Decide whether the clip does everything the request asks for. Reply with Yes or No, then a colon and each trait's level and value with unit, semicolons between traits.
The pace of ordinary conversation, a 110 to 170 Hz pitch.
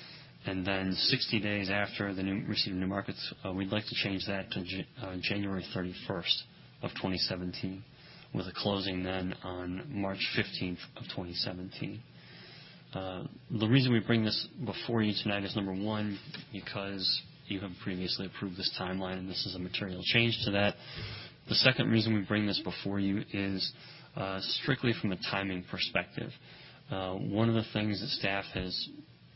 No: average, 170 wpm; low, 100 Hz